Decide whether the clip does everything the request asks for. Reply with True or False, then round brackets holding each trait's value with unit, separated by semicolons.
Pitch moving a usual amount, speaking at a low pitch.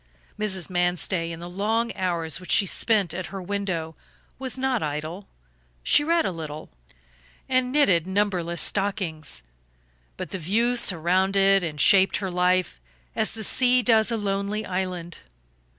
False (3.7 semitones; 190 Hz)